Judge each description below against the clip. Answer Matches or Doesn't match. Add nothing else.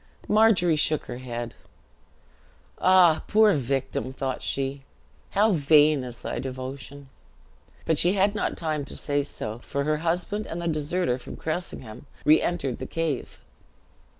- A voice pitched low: Doesn't match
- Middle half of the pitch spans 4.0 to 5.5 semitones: Matches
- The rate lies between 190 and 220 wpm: Doesn't match